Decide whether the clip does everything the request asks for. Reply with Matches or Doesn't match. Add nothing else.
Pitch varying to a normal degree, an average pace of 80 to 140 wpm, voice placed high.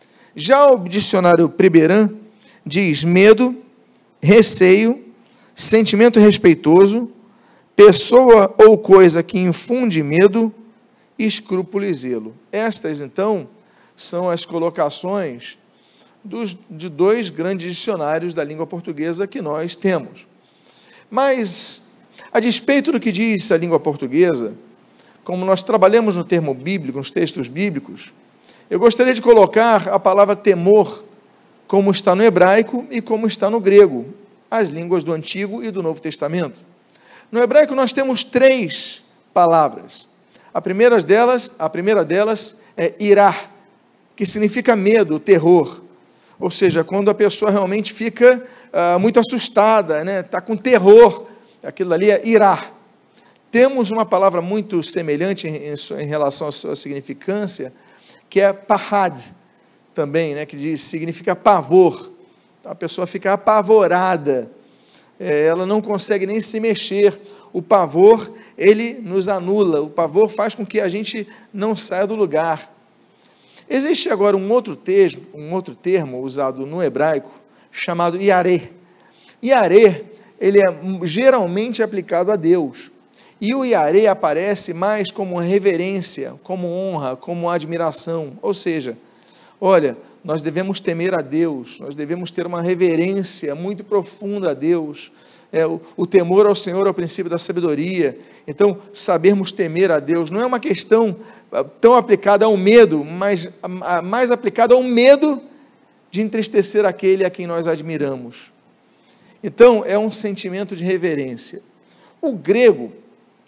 Matches